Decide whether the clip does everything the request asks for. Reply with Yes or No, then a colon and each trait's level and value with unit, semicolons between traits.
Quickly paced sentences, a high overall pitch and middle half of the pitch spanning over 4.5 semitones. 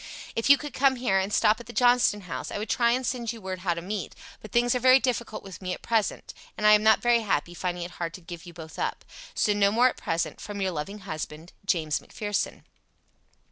Yes: fast, 245 wpm; high, 205 Hz; average, 5.0 semitones